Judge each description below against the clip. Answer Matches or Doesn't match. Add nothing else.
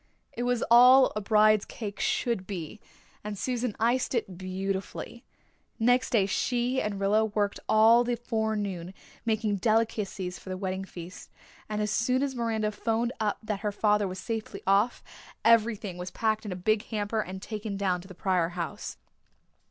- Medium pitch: Doesn't match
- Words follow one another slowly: Doesn't match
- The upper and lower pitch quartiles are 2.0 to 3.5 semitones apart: Matches